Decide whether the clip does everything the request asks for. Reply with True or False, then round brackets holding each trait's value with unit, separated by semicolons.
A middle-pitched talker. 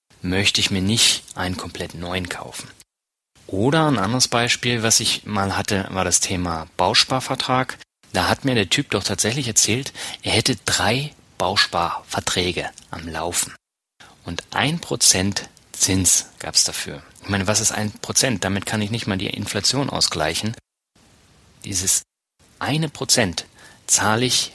False (105 Hz)